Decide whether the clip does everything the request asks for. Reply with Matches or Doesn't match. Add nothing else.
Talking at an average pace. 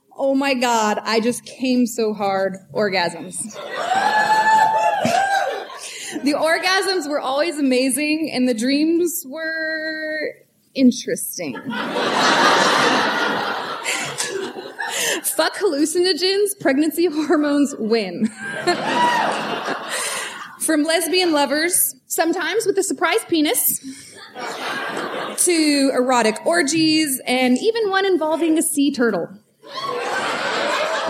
Doesn't match